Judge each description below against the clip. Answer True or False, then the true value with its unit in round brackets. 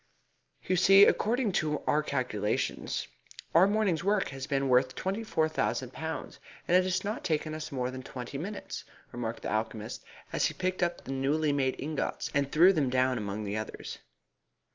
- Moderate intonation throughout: False (6.1 semitones)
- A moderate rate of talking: True (180 wpm)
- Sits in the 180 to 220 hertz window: False (150 Hz)